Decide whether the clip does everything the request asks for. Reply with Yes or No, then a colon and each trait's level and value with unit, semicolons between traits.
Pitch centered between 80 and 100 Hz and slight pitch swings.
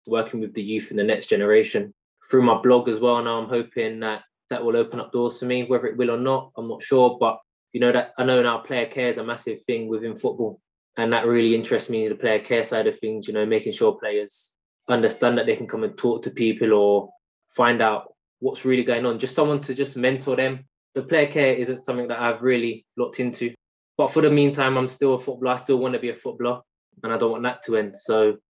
No: low, 125 Hz; narrow, 2.2 semitones